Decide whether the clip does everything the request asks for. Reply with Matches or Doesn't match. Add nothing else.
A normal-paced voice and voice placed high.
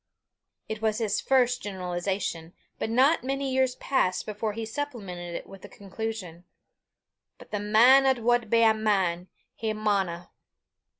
Matches